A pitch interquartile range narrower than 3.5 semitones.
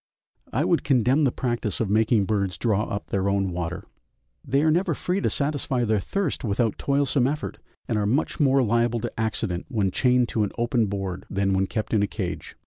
No: average, 4.6 semitones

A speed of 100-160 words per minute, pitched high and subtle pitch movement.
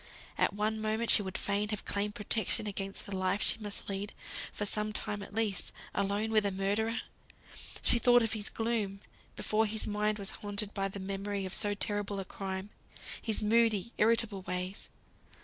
No: average, 180 wpm; high, 205 Hz; narrow, 1.6 semitones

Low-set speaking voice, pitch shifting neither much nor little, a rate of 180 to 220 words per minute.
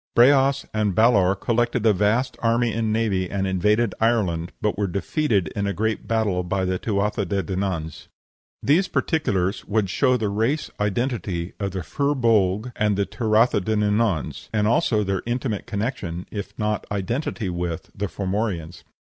No: low, 105 Hz; average, 3.3 semitones; average, 155 wpm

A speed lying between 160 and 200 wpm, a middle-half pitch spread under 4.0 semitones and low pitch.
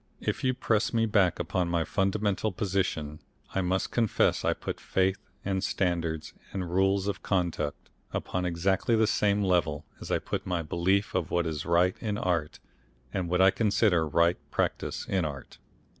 Yes: average, 170 wpm; average, 2.7 semitones; very low, 90 Hz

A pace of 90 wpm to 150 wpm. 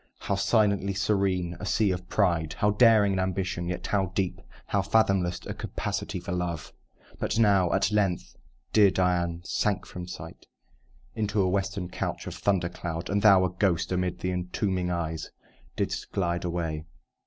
No: average, 165 wpm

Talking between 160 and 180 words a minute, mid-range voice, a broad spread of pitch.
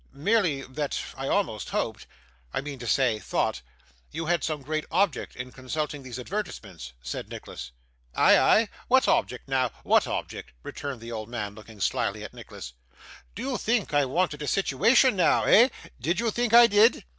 Yes: average, 170 wpm; medium, 145 Hz; wide, 8.4 semitones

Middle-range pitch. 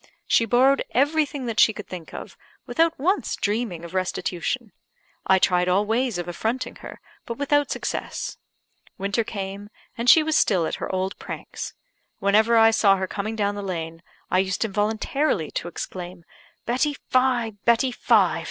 No: high, 215 Hz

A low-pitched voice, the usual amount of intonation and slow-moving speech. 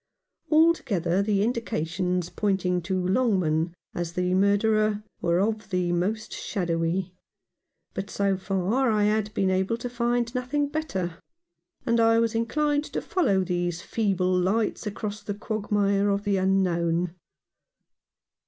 No: high, 200 Hz; average, 3.7 semitones; slow, 130 wpm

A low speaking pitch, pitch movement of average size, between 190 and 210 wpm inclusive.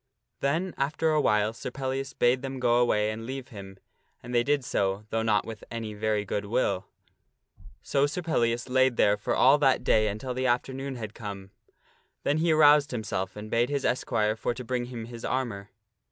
Yes: low, 120 Hz; average, 3.8 semitones; average, 195 wpm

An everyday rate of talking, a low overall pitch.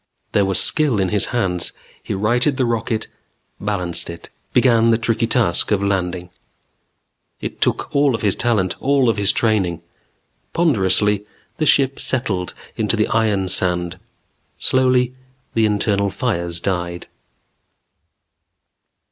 No: slow, 130 wpm; low, 105 Hz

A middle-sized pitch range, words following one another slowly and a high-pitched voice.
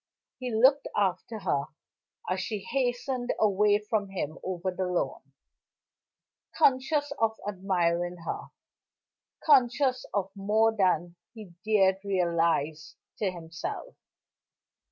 Yes: average, 4.1 semitones; slow, 105 wpm; high, 195 Hz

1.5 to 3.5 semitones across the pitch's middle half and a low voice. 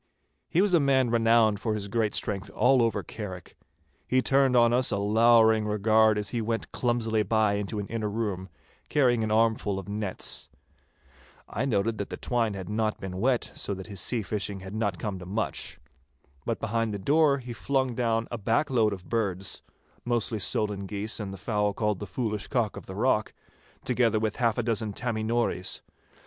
Yes: narrow, 2.6 semitones; low, 110 Hz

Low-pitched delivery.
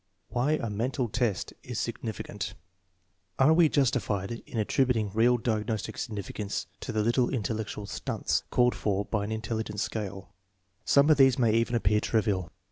Yes: low, 110 Hz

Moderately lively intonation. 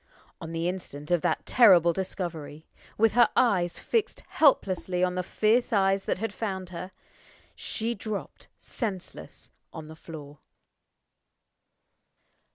Yes: average, 4.2 semitones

